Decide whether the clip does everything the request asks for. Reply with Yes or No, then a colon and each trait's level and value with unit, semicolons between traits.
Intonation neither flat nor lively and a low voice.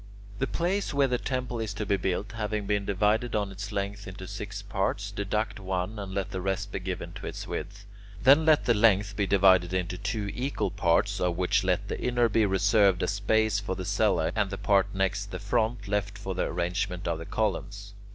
No: narrow, 2.0 semitones; low, 100 Hz